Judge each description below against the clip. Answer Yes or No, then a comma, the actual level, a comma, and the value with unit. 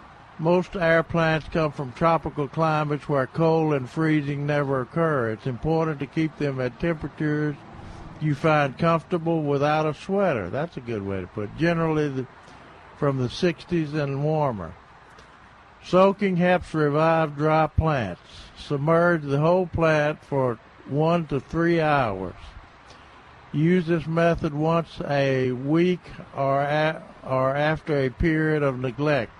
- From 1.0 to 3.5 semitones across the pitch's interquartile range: Yes, average, 3.1 semitones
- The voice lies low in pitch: No, medium, 150 Hz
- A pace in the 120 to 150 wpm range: Yes, average, 140 wpm